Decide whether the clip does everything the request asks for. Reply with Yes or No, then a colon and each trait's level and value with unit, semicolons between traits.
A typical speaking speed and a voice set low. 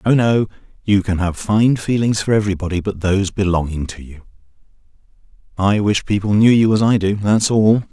Yes: average, 175 wpm; low, 100 Hz